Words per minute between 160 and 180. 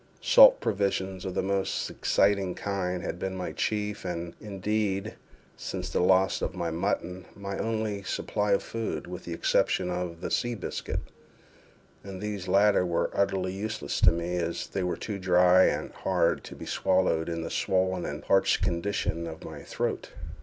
Yes: average, 170 wpm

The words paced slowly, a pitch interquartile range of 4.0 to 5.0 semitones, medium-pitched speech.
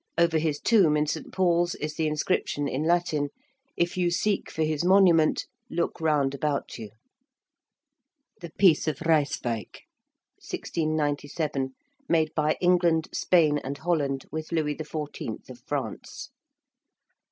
No: slow, 130 wpm; narrow, 2.6 semitones; medium, 155 Hz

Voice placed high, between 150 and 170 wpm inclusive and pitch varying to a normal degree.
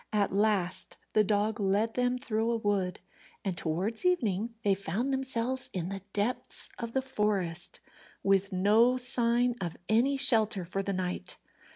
Yes: high, 215 Hz; average, 155 wpm; average, 3.7 semitones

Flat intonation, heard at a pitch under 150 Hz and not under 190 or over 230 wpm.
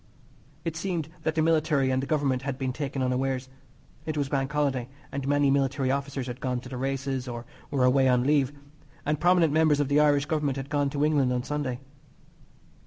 Yes: narrow, 2.2 semitones; medium, 140 Hz; average, 200 wpm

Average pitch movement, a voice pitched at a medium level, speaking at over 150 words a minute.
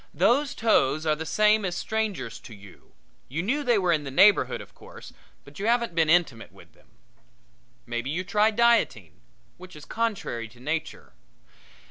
No: wide, 7.3 semitones; medium, 175 Hz; average, 170 wpm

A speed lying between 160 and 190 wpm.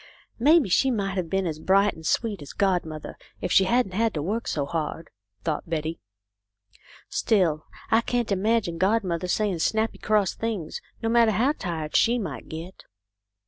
Yes: average, 175 wpm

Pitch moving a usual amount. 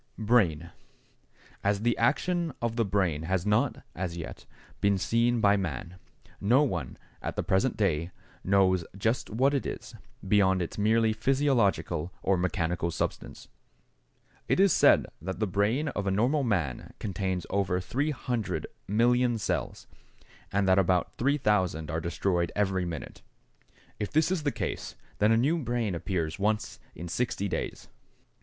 Yes: average, 4.7 semitones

